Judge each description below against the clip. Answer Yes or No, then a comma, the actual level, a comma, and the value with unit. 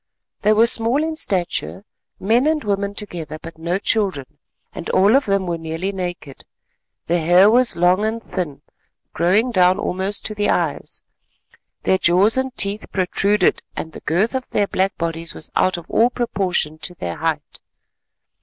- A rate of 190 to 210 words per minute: No, average, 165 wpm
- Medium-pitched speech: No, high, 195 Hz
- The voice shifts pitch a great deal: No, average, 3.8 semitones